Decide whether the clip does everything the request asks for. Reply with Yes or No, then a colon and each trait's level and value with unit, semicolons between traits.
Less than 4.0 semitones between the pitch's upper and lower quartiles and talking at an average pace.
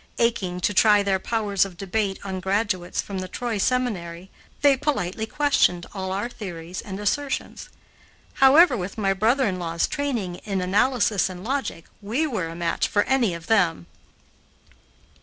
No: average, 4.4 semitones; average, 160 wpm